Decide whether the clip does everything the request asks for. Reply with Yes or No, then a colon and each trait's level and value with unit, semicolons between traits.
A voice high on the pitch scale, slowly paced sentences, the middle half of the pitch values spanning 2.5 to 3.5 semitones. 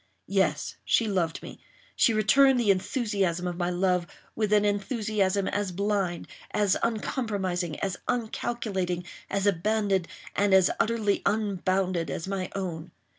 Yes: high, 195 Hz; slow, 110 wpm; average, 2.9 semitones